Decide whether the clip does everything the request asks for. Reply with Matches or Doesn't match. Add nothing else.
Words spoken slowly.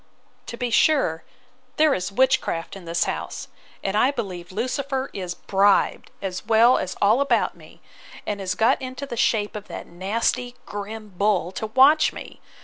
Doesn't match